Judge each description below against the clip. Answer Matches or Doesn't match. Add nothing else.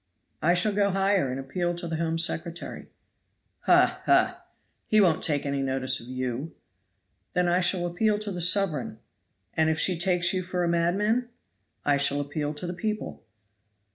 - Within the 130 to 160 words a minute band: Doesn't match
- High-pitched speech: Doesn't match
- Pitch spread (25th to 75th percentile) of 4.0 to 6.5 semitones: Matches